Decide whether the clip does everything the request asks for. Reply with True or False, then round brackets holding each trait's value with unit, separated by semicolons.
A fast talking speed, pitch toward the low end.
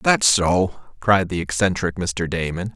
False (150 wpm; 95 Hz)